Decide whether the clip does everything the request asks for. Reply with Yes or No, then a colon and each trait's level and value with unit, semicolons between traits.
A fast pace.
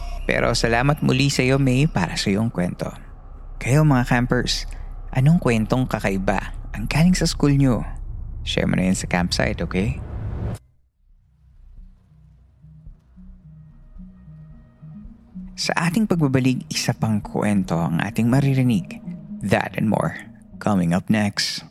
No: average, 120 wpm